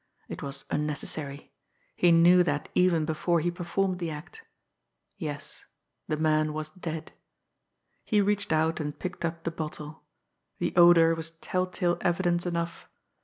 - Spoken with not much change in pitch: Yes, narrow, 2.2 semitones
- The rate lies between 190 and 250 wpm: No, average, 145 wpm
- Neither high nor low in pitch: Yes, medium, 165 Hz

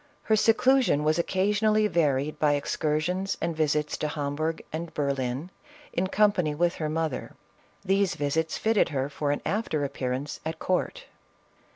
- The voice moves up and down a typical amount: Yes, average, 4.6 semitones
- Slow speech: No, average, 150 wpm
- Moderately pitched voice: Yes, medium, 160 Hz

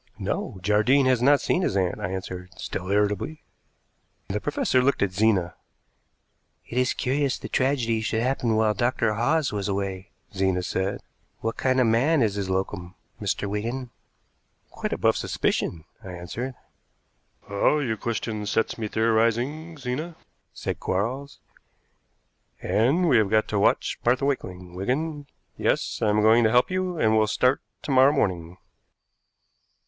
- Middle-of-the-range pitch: No, low, 110 Hz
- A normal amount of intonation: Yes, average, 4.7 semitones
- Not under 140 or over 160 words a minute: Yes, average, 150 wpm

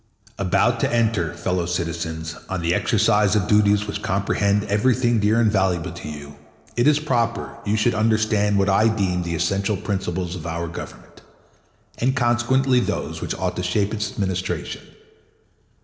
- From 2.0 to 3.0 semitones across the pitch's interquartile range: No, average, 3.8 semitones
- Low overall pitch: Yes, low, 100 Hz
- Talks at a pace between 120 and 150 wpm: No, average, 165 wpm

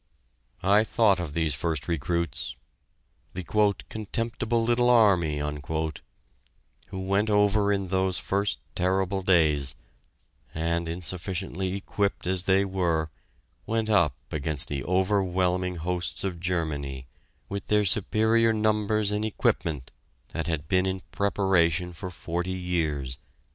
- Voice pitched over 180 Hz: No, very low, 95 Hz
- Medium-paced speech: No, slow, 115 wpm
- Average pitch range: Yes, average, 3.3 semitones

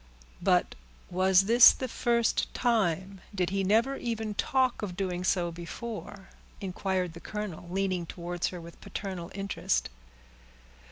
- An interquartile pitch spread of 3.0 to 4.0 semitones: Yes, average, 3.4 semitones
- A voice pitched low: No, high, 190 Hz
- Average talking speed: No, slow, 130 wpm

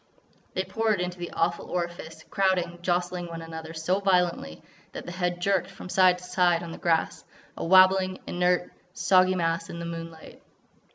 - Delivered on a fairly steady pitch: Yes, narrow, 1.7 semitones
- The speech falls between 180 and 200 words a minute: No, average, 170 wpm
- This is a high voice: No, medium, 180 Hz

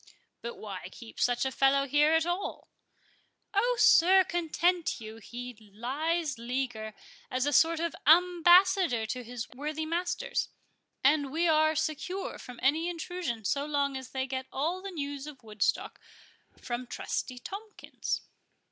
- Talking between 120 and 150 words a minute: Yes, average, 140 wpm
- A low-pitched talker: No, very high, 290 Hz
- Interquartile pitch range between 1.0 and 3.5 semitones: No, average, 5.3 semitones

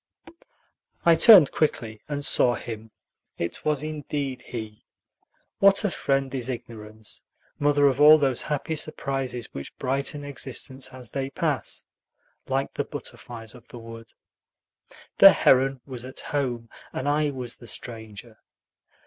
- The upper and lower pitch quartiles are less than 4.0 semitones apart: Yes, average, 3.6 semitones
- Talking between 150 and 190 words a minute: No, slow, 135 wpm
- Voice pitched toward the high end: No, low, 130 Hz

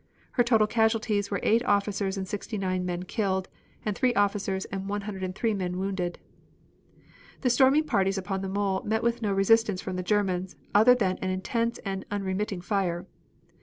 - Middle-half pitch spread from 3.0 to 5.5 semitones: No, narrow, 2.5 semitones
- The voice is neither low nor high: No, high, 200 Hz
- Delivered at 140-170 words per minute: Yes, average, 165 wpm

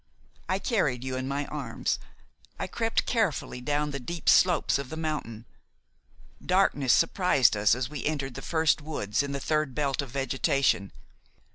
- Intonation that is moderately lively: Yes, average, 3.4 semitones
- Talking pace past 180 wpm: No, average, 160 wpm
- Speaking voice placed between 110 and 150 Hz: Yes, medium, 140 Hz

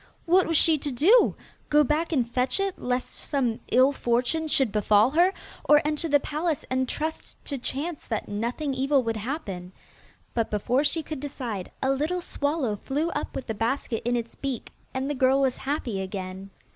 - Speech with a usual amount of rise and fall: Yes, average, 4.3 semitones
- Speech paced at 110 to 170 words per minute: No, average, 185 wpm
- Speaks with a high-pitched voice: Yes, very high, 270 Hz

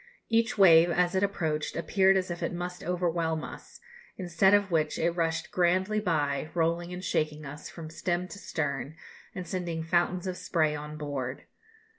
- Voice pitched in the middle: Yes, medium, 170 Hz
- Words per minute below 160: No, average, 170 wpm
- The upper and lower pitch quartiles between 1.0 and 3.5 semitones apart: Yes, narrow, 2.5 semitones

